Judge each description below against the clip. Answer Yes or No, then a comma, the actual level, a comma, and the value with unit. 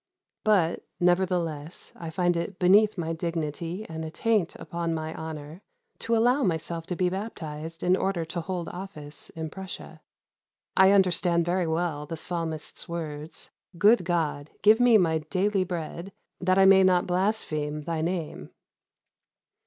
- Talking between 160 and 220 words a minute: No, average, 145 wpm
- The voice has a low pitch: No, medium, 175 Hz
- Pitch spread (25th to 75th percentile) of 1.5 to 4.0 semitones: Yes, average, 2.8 semitones